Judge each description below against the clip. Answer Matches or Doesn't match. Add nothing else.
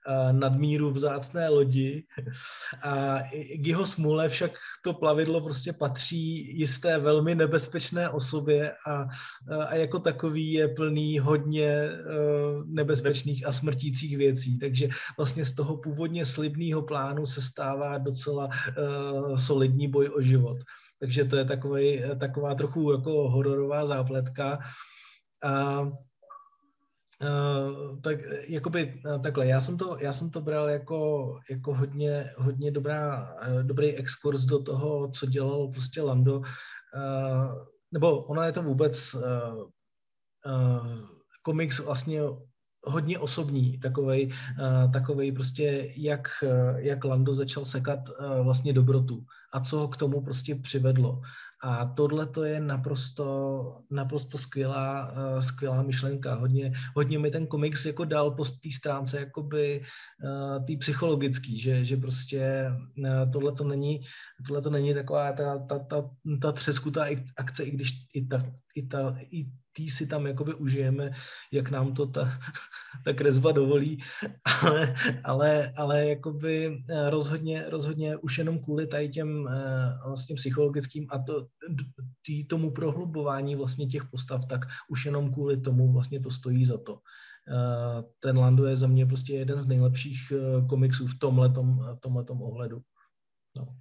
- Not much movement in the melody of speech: Matches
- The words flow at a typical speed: Matches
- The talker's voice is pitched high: Doesn't match